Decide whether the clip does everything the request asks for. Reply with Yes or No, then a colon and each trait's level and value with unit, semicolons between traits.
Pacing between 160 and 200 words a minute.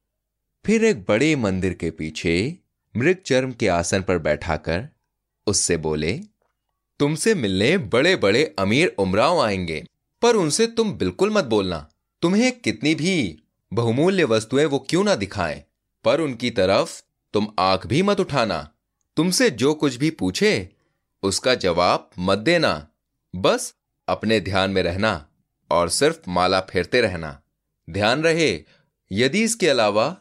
No: average, 135 wpm